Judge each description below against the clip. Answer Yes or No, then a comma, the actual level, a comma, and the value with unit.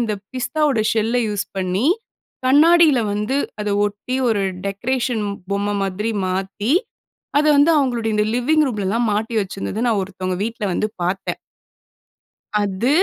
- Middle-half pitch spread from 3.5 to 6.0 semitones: Yes, average, 4.2 semitones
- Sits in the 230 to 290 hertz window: No, high, 220 Hz